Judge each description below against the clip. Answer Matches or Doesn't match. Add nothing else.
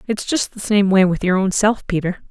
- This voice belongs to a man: Doesn't match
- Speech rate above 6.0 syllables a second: Doesn't match